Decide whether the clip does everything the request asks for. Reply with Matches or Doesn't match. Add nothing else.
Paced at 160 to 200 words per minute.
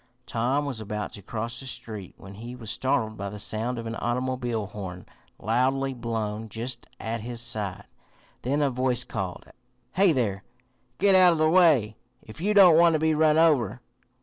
Matches